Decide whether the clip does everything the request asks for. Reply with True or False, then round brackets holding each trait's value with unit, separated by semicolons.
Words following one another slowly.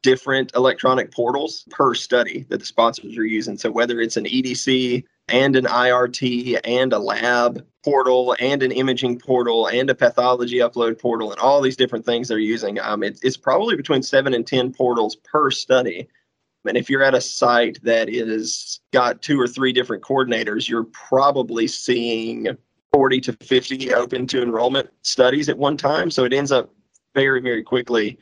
False (175 wpm)